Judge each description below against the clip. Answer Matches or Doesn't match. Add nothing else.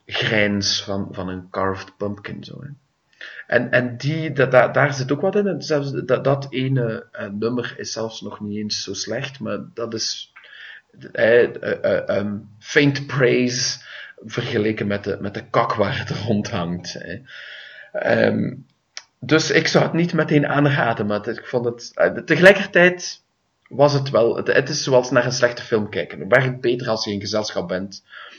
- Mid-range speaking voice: Doesn't match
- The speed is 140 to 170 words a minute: Doesn't match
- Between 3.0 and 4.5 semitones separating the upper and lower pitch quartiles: Doesn't match